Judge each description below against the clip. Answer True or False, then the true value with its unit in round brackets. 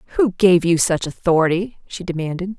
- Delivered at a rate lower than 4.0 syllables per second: False (5.5 syllables/s)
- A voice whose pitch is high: False (180 Hz)